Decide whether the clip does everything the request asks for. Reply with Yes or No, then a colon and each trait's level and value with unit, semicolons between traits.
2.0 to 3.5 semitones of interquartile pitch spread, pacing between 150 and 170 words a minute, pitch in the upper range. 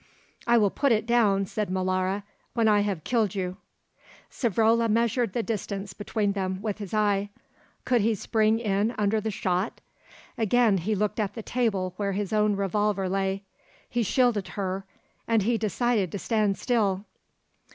Yes: narrow, 2.5 semitones; average, 160 wpm; high, 210 Hz